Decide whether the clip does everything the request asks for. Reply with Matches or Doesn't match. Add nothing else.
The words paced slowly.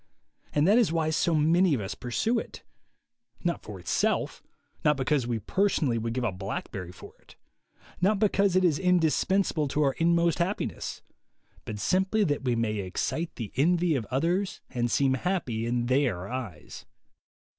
Doesn't match